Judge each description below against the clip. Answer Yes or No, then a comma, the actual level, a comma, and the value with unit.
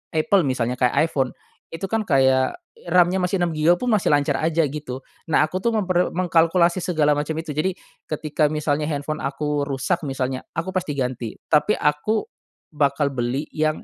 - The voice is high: No, medium, 155 Hz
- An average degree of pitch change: Yes, average, 3.9 semitones